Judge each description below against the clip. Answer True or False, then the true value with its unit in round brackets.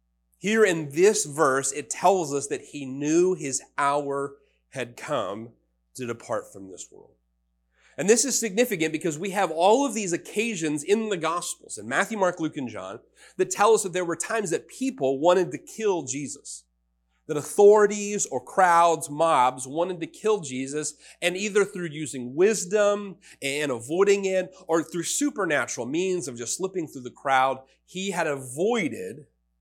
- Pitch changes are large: True (6.6 semitones)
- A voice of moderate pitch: True (165 Hz)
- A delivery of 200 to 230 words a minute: False (165 wpm)